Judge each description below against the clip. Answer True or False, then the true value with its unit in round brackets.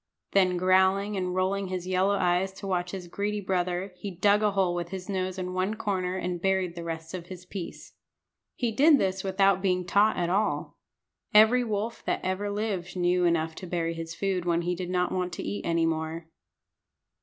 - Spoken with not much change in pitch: True (2.0 semitones)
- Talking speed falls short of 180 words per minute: False (200 wpm)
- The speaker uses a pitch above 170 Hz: True (185 Hz)